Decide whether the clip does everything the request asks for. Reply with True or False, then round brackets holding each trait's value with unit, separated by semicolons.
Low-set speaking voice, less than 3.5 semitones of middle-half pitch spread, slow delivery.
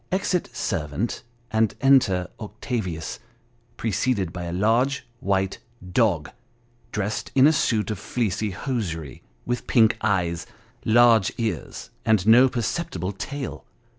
False (110 Hz; 4.8 semitones; 115 wpm)